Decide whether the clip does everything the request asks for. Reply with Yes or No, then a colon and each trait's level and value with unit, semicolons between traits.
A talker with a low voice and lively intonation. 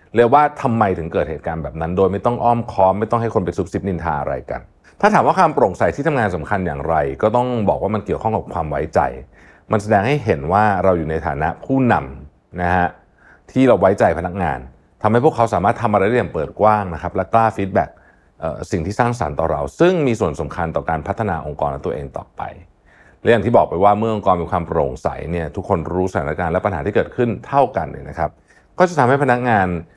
Yes: low, 100 Hz; wide, 5.7 semitones